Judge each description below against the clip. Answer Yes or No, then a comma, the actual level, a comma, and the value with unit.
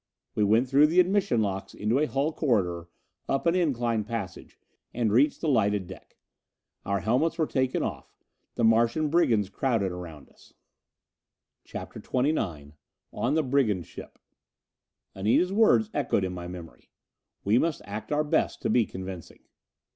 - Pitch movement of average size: No, wide, 7.0 semitones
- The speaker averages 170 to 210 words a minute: No, average, 150 wpm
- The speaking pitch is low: Yes, low, 115 Hz